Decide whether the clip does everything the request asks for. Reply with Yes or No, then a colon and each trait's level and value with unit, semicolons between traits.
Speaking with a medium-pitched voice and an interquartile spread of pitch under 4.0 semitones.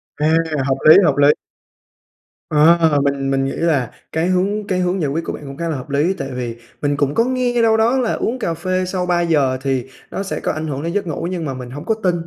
No: medium, 160 Hz; average, 4.8 semitones